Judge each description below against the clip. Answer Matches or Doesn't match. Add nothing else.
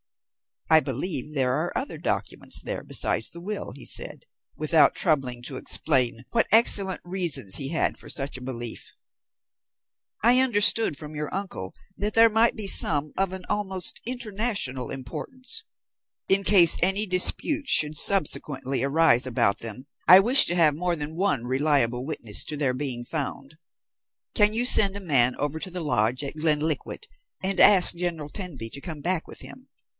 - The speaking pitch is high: Doesn't match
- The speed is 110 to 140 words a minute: Doesn't match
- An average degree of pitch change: Doesn't match